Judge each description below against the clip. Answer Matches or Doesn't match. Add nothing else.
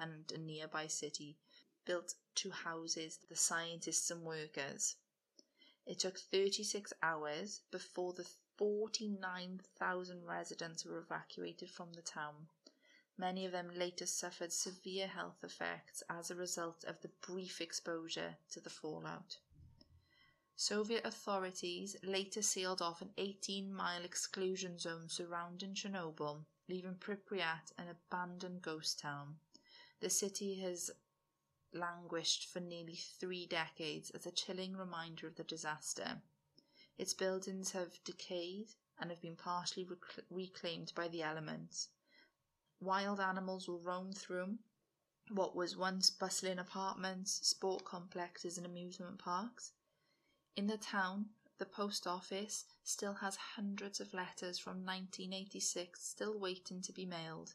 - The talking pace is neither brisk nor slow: Doesn't match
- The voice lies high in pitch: Doesn't match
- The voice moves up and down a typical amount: Doesn't match